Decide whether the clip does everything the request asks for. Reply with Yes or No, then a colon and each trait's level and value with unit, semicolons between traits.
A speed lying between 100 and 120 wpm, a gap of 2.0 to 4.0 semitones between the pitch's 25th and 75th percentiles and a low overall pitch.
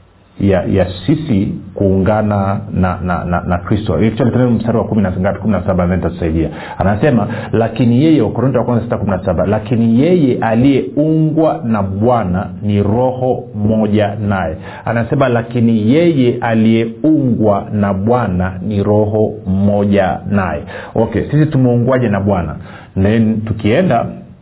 Yes: average, 115 wpm; average, 3.5 semitones; low, 110 Hz